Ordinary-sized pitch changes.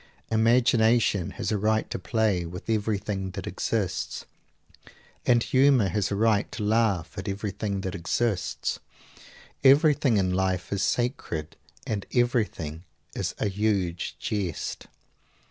Yes: average, 3.2 semitones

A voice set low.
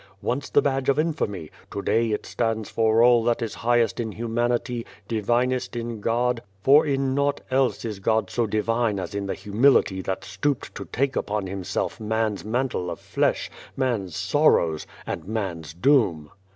Yes: low, 115 Hz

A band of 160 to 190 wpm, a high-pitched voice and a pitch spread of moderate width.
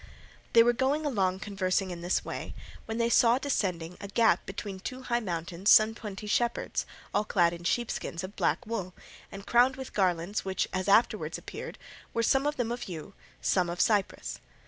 Yes: average, 185 wpm; high, 205 Hz; average, 4.4 semitones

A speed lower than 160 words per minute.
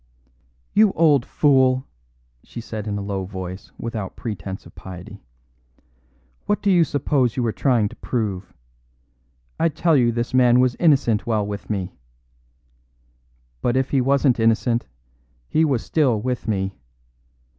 Yes: average, 145 wpm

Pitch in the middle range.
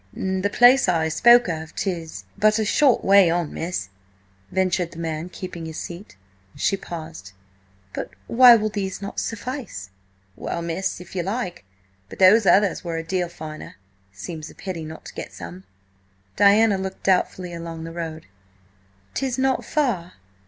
Yes: medium, 180 Hz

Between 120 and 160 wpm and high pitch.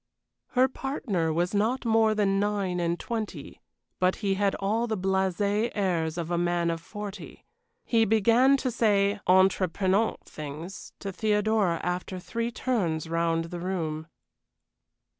Yes: average, 140 wpm; high, 195 Hz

